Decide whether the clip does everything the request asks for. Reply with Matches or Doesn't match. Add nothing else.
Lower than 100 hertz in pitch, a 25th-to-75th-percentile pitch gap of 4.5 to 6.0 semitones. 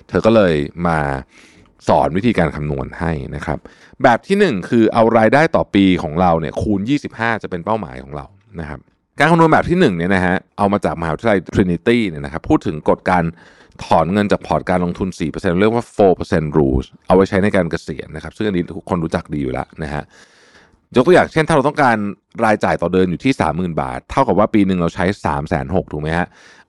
Matches